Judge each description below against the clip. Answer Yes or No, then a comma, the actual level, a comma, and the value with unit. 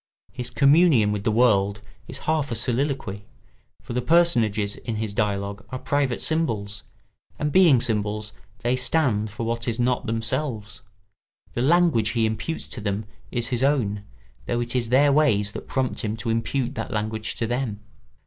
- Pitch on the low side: Yes, low, 115 Hz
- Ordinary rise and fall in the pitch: Yes, average, 3.9 semitones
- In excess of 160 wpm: Yes, average, 170 wpm